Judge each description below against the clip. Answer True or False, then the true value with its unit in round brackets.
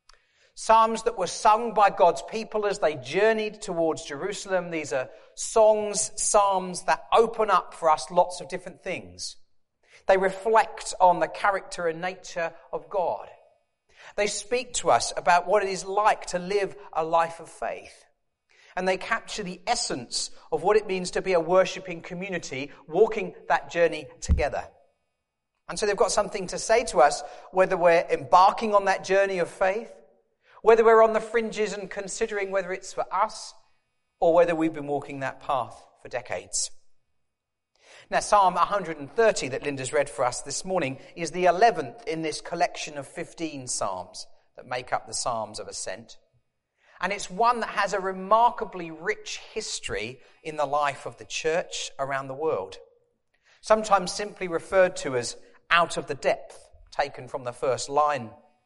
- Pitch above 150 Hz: True (185 Hz)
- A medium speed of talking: True (165 wpm)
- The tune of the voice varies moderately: True (4.6 semitones)